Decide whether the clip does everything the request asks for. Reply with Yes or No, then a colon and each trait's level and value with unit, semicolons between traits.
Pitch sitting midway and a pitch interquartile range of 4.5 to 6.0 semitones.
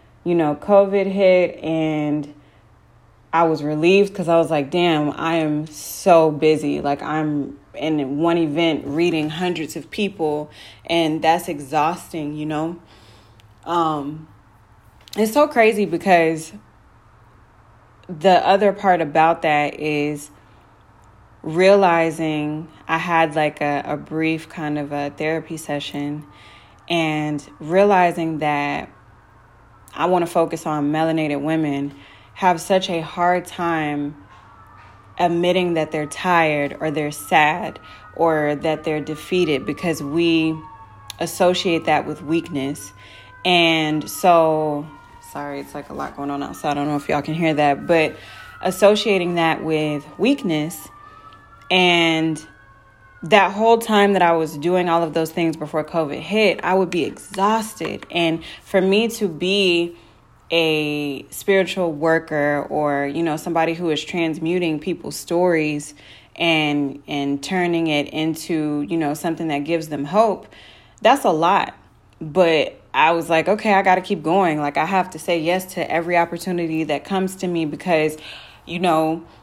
No: medium, 160 Hz; average, 2.9 semitones